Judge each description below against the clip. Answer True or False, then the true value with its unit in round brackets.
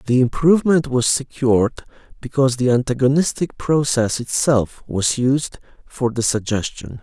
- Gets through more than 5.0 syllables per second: False (4.7 syllables/s)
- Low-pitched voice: True (130 Hz)